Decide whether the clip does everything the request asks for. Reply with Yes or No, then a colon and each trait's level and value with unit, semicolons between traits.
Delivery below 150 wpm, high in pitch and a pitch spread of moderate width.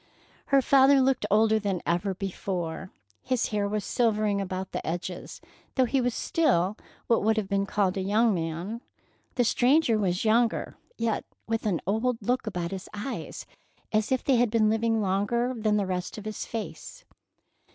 No: average, 170 wpm; high, 215 Hz; average, 3.6 semitones